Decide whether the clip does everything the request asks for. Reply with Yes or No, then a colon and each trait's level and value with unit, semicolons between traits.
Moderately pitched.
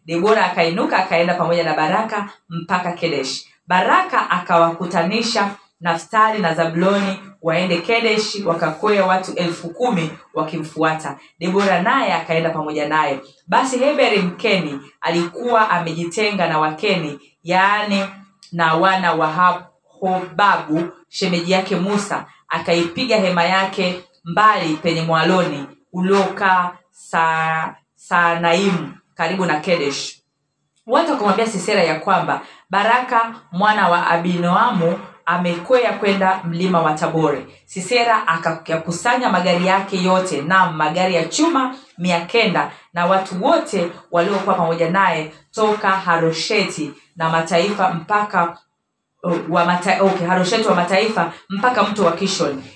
Yes: medium, 180 Hz